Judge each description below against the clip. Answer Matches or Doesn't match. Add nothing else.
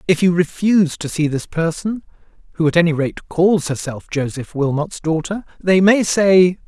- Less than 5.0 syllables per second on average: Matches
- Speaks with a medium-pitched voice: Matches